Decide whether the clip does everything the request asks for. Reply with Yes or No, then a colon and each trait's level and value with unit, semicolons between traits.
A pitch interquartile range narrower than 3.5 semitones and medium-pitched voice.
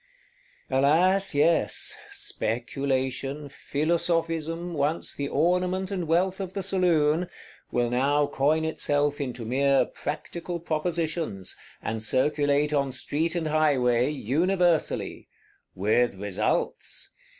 No: average, 4.0 semitones; medium, 150 Hz